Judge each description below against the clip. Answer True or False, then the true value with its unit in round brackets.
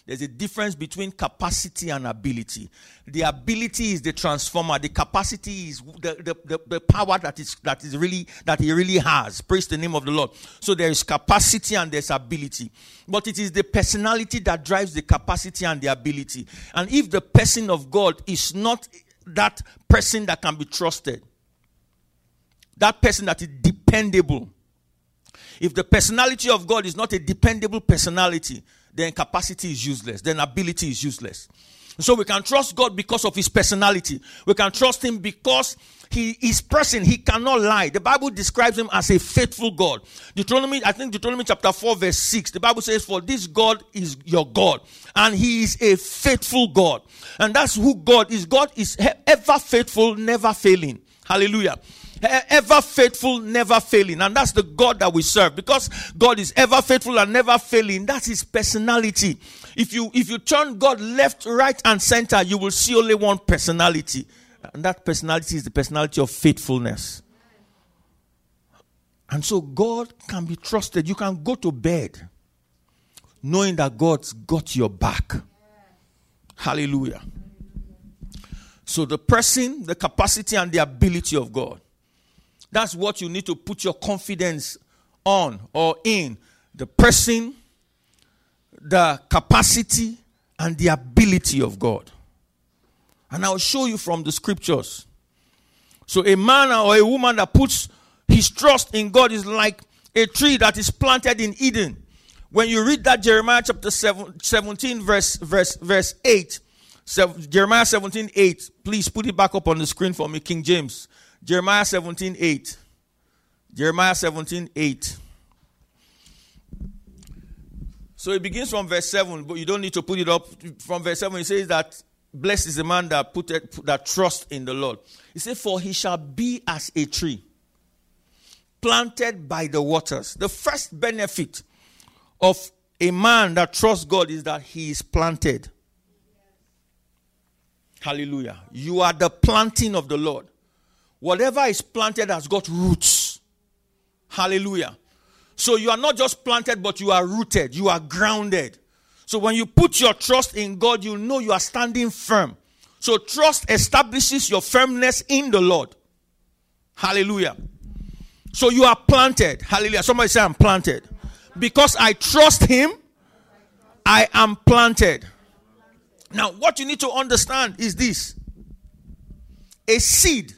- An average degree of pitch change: False (6.6 semitones)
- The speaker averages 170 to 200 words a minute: False (160 wpm)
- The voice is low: False (190 Hz)